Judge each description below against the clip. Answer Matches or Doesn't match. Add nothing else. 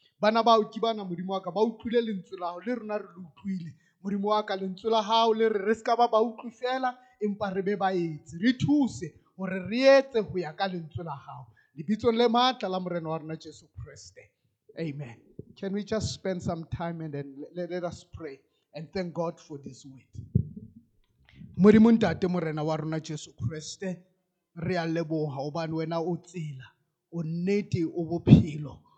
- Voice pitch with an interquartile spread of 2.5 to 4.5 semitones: Doesn't match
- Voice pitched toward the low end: Doesn't match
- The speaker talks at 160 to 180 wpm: Doesn't match